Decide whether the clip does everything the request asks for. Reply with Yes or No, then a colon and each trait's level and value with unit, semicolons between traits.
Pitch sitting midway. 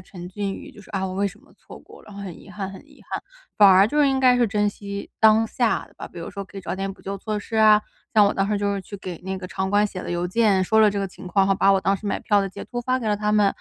No: high, 200 Hz